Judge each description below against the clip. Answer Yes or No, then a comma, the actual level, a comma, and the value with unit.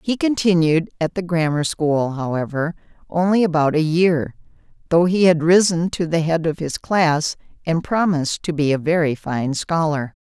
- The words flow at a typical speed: Yes, average, 170 wpm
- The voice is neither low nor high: Yes, medium, 165 Hz